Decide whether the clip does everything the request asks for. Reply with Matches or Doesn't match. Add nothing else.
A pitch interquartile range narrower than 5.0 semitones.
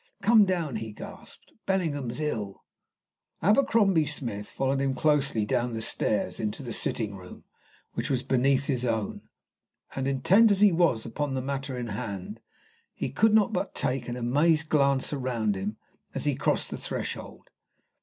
Doesn't match